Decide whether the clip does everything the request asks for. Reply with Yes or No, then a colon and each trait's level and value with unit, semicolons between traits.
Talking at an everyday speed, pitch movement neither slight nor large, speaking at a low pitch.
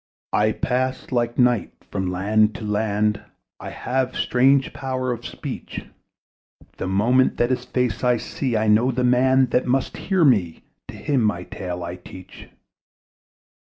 Yes: average, 155 wpm; average, 3.6 semitones; low, 120 Hz